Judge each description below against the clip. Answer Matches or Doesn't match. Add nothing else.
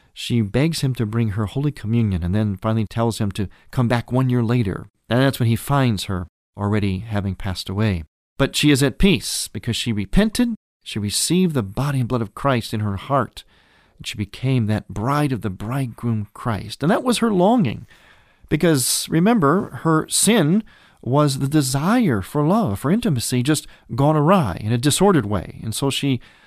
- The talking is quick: Doesn't match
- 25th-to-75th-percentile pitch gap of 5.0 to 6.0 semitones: Matches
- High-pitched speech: Doesn't match